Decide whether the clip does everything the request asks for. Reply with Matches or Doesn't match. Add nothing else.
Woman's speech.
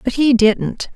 Matches